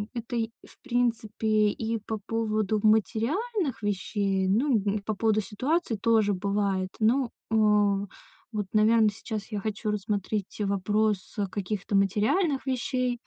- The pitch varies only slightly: Yes, narrow, 2.1 semitones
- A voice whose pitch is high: Yes, high, 215 Hz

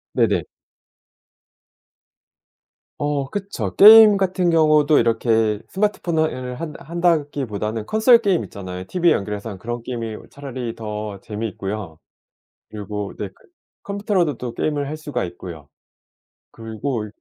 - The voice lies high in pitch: No, low, 125 Hz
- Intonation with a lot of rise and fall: Yes, wide, 7.7 semitones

